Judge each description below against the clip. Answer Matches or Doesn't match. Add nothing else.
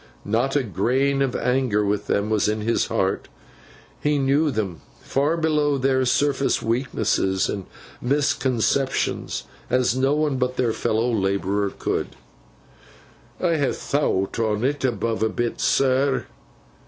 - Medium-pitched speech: Doesn't match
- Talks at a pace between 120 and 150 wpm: Matches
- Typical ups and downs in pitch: Matches